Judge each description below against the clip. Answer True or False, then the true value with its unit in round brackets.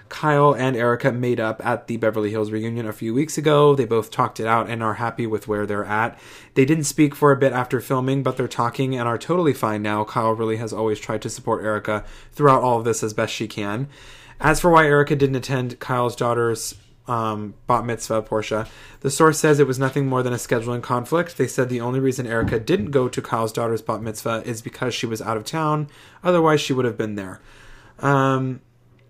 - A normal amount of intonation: True (3.4 semitones)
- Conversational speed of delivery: False (225 wpm)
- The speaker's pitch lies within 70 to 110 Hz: False (120 Hz)